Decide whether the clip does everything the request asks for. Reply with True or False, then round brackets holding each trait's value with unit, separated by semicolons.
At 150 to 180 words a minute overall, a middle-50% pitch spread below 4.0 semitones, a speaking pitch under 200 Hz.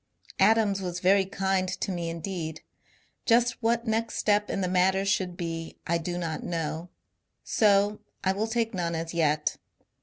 True (160 wpm; 3.5 semitones; 185 Hz)